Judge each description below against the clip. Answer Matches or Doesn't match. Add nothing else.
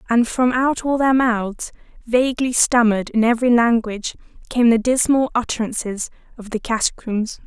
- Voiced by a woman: Matches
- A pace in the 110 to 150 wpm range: Matches